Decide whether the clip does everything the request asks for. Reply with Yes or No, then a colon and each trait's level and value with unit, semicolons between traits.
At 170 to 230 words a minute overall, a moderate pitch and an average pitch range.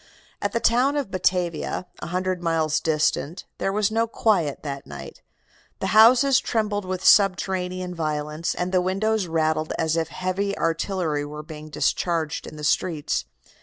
No: average, 155 wpm; medium, 180 Hz; average, 4.2 semitones